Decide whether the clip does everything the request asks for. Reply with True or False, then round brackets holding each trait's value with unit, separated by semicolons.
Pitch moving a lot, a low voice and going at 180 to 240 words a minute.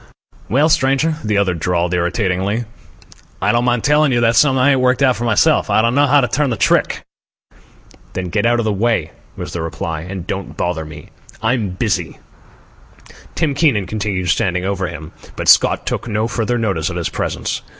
True (5.8 semitones; 110 Hz; 190 wpm)